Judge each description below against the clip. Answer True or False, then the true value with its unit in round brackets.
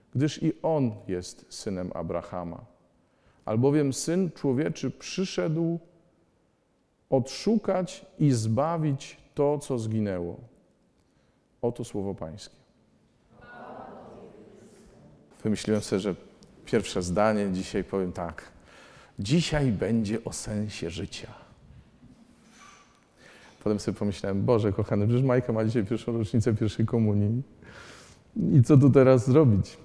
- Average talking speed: False (100 wpm)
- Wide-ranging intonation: True (5.8 semitones)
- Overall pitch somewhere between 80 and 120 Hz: True (115 Hz)